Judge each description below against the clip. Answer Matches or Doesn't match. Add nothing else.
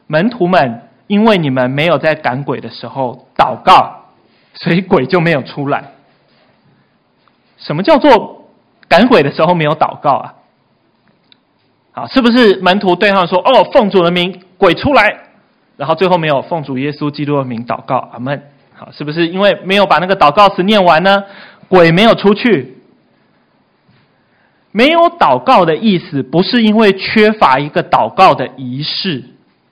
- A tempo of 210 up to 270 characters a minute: Matches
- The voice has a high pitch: Doesn't match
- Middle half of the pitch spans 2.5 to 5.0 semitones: Doesn't match